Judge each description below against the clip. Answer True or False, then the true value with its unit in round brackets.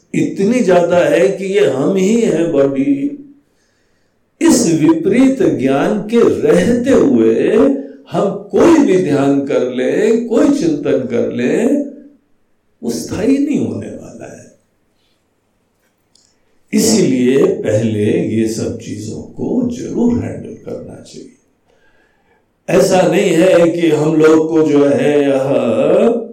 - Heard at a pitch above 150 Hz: True (190 Hz)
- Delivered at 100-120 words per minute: True (110 wpm)